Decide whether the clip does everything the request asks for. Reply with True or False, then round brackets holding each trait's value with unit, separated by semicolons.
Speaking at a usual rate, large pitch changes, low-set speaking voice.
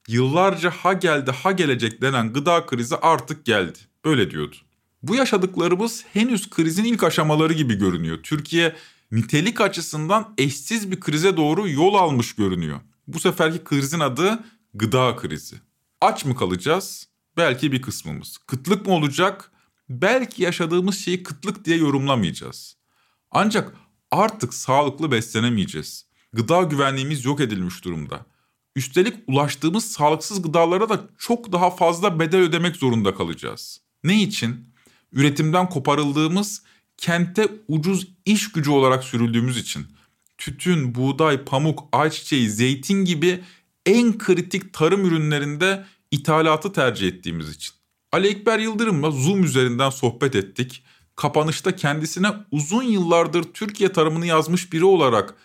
False (120 wpm; 6.1 semitones; 160 Hz)